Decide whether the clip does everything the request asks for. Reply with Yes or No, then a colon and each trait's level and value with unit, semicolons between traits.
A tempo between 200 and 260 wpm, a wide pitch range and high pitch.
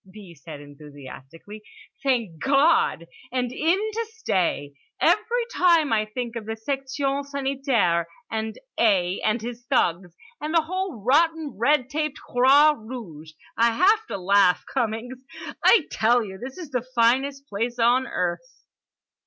No: average, 140 wpm; wide, 6.1 semitones; high, 245 Hz